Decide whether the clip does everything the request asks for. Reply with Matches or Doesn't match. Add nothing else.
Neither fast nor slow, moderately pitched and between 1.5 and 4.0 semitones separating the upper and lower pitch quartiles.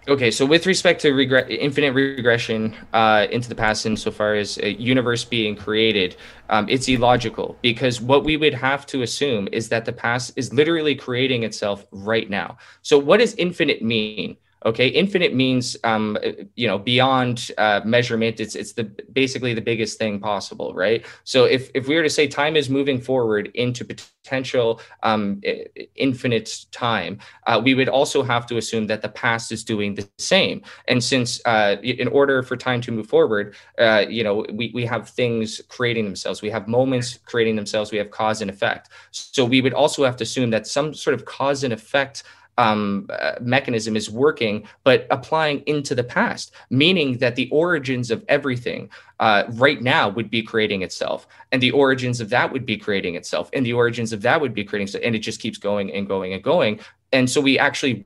Doesn't match